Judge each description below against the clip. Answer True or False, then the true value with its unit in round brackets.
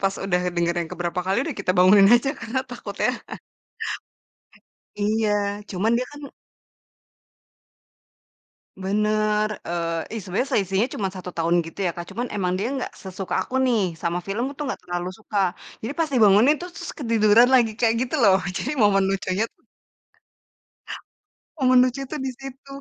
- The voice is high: True (210 Hz)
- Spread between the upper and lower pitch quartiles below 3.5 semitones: False (4.6 semitones)